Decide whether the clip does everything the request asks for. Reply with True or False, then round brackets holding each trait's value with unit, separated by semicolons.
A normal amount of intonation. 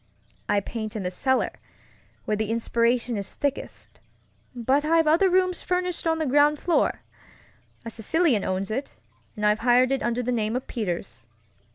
False (5.8 semitones)